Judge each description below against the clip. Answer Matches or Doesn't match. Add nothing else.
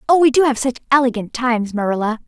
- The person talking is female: Matches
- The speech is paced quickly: Matches